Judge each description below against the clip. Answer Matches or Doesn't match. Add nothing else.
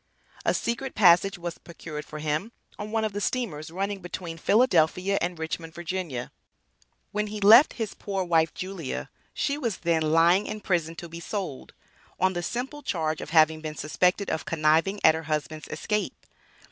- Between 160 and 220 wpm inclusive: Matches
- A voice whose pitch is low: Doesn't match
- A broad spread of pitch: Doesn't match